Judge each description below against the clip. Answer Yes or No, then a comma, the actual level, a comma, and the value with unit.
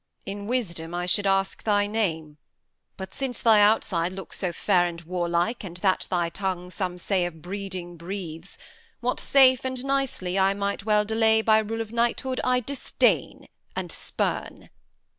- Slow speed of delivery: No, average, 165 wpm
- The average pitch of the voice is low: No, high, 195 Hz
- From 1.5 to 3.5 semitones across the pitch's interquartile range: No, average, 4.0 semitones